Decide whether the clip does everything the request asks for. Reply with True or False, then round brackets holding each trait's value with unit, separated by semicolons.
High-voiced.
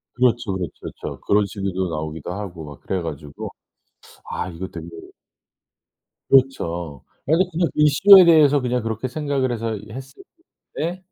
False (110 Hz)